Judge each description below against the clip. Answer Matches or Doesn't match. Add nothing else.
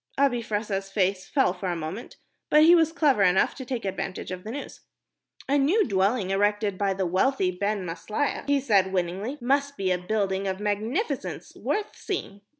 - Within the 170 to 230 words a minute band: Matches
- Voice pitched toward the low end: Doesn't match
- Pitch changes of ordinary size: Doesn't match